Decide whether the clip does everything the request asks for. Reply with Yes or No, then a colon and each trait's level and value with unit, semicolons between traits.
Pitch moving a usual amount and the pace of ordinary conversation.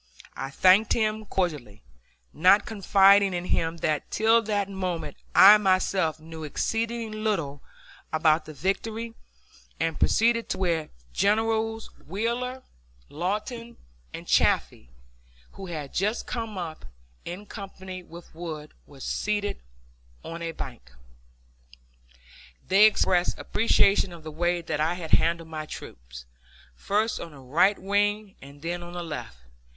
No: average, 4.7 semitones; slow, 130 wpm